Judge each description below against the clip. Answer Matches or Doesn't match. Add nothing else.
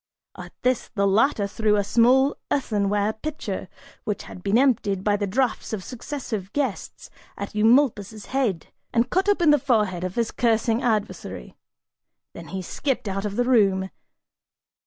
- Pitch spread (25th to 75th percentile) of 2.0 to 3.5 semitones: Doesn't match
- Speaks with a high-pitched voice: Matches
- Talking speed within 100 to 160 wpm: Matches